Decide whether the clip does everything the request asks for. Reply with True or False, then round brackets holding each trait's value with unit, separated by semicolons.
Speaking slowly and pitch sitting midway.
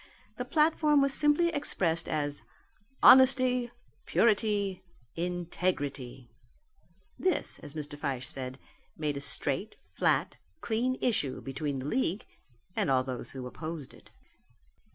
True (110 wpm; 170 Hz)